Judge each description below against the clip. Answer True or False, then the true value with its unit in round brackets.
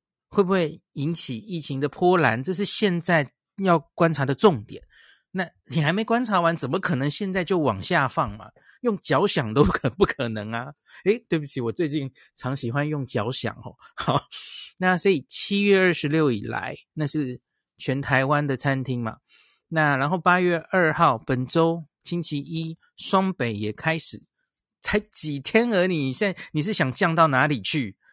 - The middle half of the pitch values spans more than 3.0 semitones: True (5.2 semitones)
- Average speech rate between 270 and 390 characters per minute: False (245 characters per minute)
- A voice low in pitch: False (155 Hz)